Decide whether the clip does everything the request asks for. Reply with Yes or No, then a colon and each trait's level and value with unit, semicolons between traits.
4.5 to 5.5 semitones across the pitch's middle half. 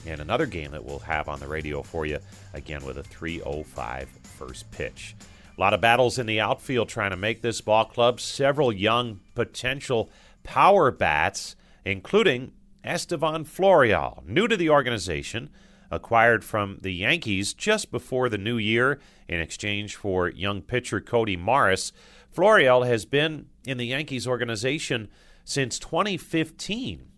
Yes: average, 5.2 semitones